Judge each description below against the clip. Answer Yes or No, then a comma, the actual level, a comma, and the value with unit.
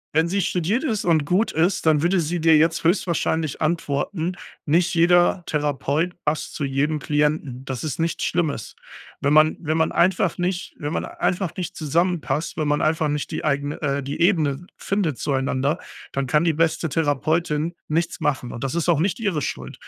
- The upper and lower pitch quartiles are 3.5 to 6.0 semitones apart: No, average, 2.9 semitones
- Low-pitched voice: No, medium, 160 Hz